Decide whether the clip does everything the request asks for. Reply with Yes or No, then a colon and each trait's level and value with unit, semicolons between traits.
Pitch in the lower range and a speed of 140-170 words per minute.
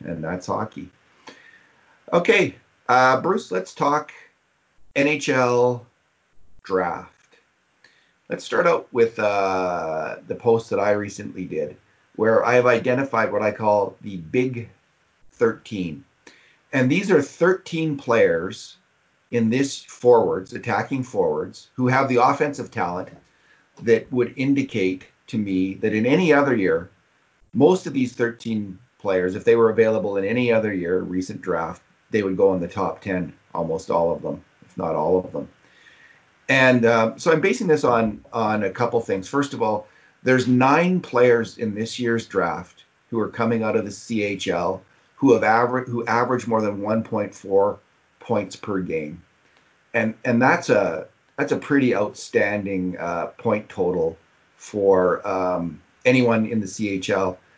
Yes: low, 115 Hz; average, 150 wpm